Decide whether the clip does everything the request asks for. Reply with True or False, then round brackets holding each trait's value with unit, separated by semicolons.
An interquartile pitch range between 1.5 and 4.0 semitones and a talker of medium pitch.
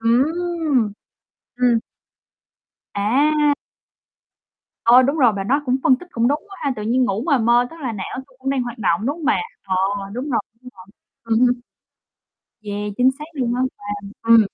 False (3.7 semitones; 250 Hz)